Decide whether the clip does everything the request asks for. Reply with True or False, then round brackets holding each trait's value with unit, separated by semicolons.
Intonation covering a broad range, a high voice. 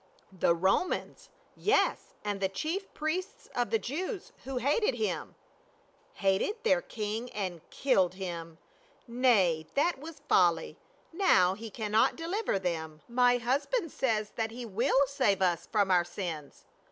True (7.8 semitones; 225 Hz)